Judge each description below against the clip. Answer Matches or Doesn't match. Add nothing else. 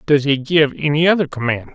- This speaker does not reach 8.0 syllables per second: Matches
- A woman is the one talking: Doesn't match